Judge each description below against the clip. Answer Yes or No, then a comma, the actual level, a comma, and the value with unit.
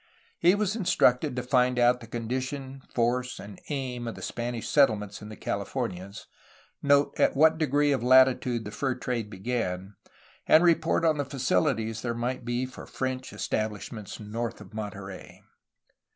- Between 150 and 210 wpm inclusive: Yes, average, 155 wpm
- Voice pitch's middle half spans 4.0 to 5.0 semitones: No, average, 3.5 semitones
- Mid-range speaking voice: No, low, 125 Hz